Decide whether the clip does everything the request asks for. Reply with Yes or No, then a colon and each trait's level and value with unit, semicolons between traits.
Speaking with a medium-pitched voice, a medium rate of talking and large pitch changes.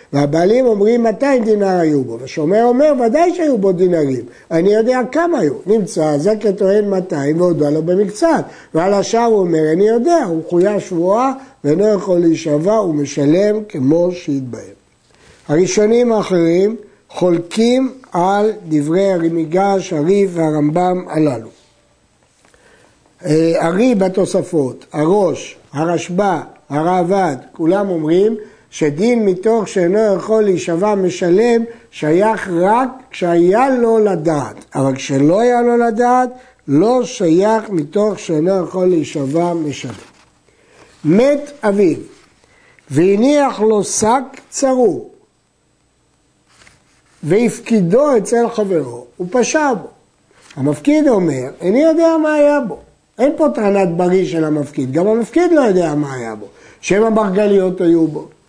No: high, 195 Hz; average, 120 wpm; wide, 5.8 semitones